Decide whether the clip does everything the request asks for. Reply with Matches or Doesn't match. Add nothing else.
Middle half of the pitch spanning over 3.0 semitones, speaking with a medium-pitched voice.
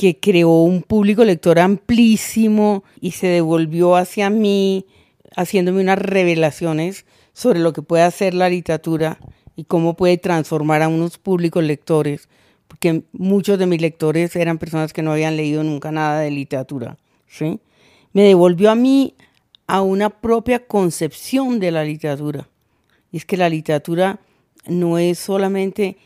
Matches